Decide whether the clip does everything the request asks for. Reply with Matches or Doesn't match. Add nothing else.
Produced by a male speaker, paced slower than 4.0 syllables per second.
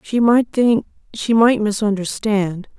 Doesn't match